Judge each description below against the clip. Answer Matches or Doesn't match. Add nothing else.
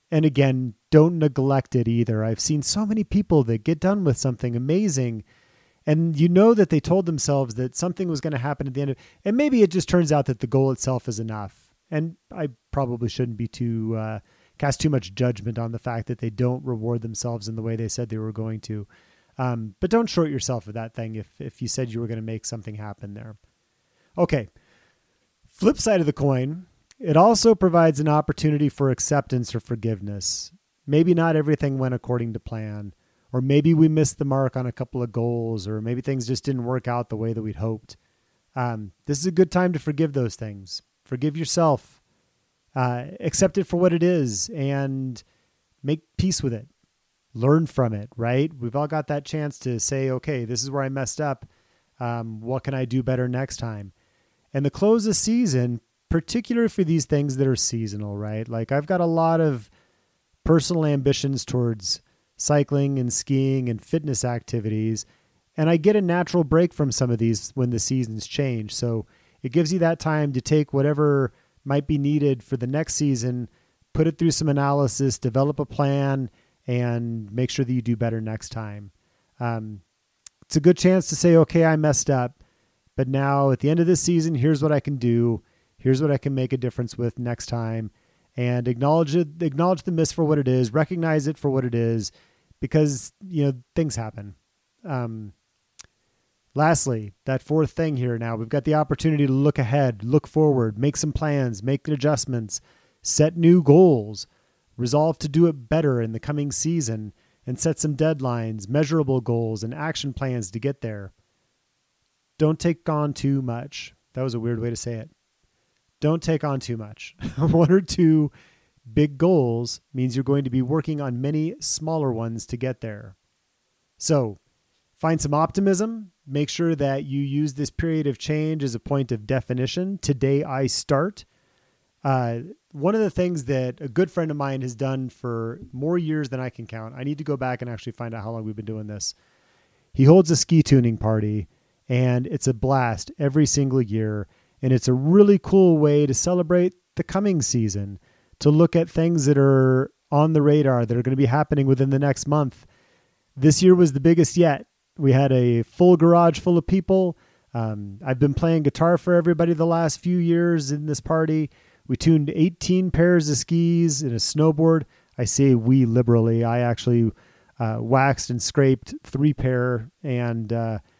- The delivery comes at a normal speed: Matches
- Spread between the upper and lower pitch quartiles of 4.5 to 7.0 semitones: Matches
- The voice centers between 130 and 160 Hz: Matches